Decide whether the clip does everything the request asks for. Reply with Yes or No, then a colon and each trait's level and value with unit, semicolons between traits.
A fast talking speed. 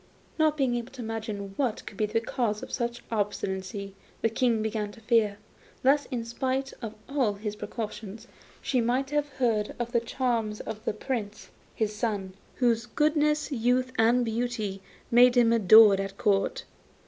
No: average, 170 wpm